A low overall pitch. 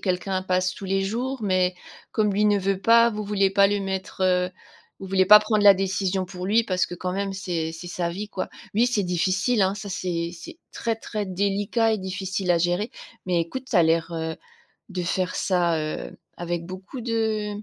No: high, 190 Hz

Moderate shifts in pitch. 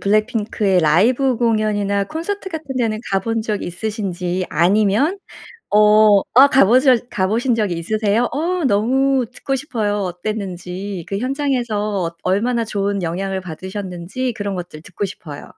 Yes: average, 4.3 semitones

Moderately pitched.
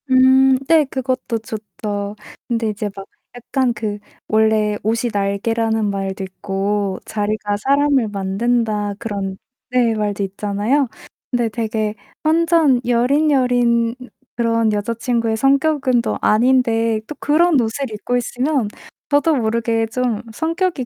No: high, 230 Hz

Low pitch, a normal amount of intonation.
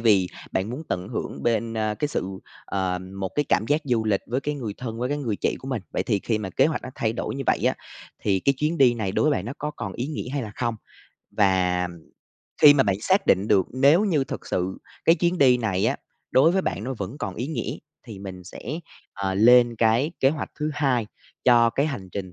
No: low, 120 Hz; wide, 5.9 semitones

